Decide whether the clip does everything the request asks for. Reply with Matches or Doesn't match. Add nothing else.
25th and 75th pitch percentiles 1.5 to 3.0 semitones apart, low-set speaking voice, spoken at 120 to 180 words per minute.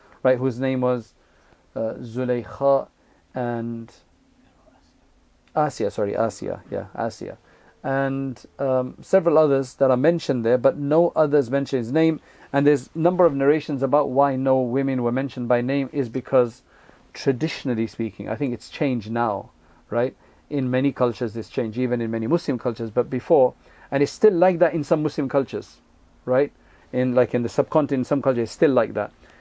Matches